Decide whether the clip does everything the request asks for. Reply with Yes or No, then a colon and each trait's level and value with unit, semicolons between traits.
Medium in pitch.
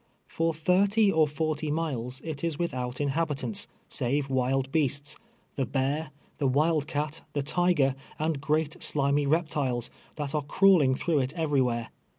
Yes: medium, 145 Hz